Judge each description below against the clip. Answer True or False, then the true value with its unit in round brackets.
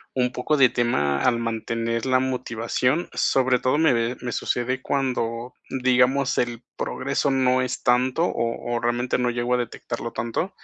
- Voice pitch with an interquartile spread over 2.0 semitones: False (1.7 semitones)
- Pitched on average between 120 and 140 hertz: True (125 Hz)